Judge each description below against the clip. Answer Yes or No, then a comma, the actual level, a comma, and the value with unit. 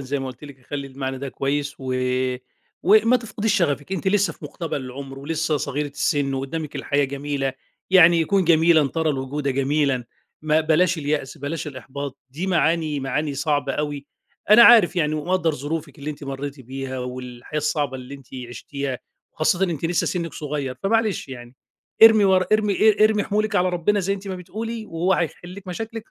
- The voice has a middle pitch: Yes, medium, 150 Hz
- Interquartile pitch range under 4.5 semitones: No, average, 4.8 semitones